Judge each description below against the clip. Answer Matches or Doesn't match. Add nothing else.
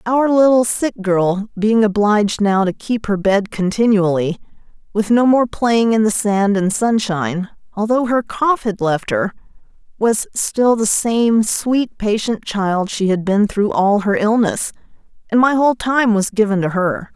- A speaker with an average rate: Matches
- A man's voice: Doesn't match